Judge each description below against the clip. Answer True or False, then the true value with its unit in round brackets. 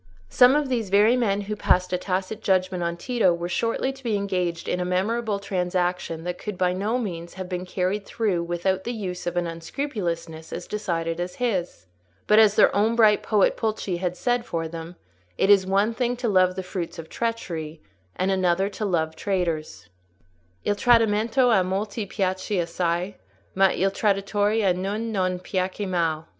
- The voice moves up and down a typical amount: True (3.2 semitones)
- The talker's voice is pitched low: False (190 Hz)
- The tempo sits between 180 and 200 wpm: True (185 wpm)